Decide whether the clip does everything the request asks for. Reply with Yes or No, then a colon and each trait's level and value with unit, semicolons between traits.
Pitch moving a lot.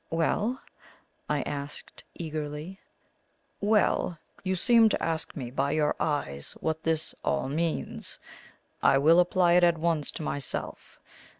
No: average, 3.1 semitones